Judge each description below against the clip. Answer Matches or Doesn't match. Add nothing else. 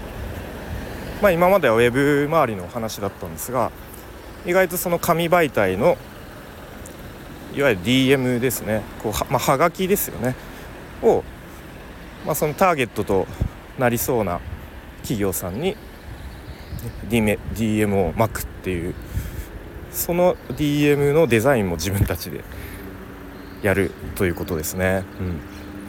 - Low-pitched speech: Matches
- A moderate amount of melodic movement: Doesn't match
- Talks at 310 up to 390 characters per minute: Doesn't match